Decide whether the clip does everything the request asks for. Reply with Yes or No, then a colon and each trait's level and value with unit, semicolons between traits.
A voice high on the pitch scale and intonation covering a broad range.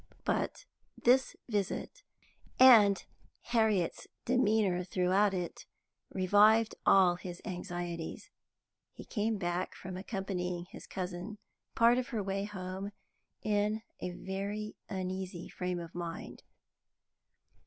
No: high, 195 Hz; average, 2.9 semitones